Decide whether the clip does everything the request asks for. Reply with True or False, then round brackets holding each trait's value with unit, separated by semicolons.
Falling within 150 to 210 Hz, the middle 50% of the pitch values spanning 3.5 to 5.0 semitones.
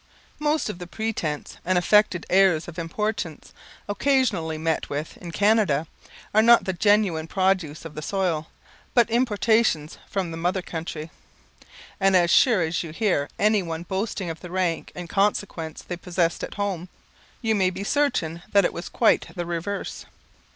True (185 Hz; 4.0 semitones)